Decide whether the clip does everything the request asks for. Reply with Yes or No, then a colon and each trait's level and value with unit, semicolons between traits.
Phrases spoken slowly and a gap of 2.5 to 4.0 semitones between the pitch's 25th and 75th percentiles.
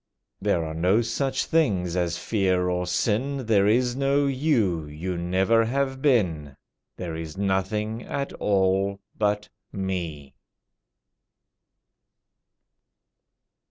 No: slow, 100 wpm; average, 5.0 semitones